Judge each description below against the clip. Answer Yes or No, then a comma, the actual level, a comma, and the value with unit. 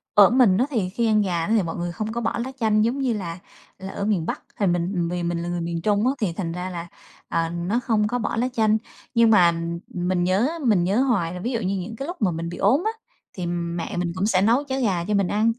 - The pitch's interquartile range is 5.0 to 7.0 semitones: No, average, 4.6 semitones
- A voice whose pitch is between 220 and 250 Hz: No, high, 195 Hz